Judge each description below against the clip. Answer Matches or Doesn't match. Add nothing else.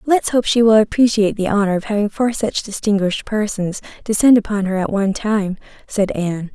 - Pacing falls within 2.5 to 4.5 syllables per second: Doesn't match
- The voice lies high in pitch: Matches